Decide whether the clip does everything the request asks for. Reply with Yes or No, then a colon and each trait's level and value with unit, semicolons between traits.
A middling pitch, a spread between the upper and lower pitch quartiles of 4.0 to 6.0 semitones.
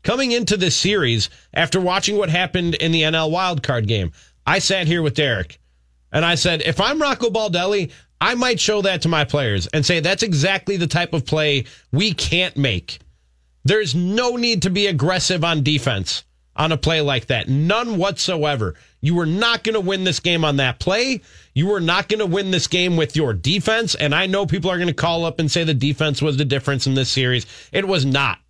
Yes: medium, 165 Hz; average, 5.3 semitones